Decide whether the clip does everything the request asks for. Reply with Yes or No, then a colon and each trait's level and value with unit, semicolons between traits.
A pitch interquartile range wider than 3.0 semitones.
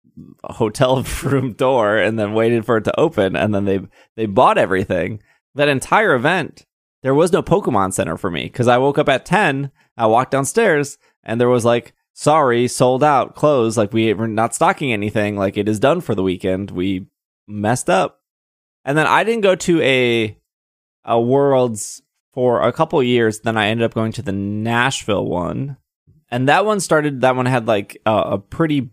Yes: average, 4.6 semitones